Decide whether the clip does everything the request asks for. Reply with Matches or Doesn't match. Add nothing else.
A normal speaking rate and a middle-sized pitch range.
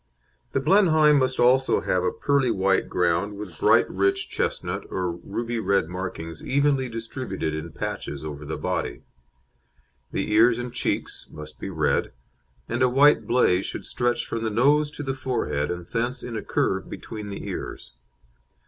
Doesn't match